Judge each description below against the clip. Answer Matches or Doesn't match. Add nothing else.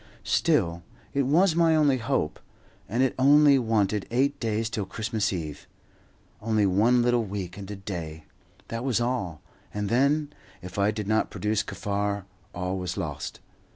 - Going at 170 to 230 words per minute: Doesn't match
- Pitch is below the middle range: Matches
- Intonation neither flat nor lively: Matches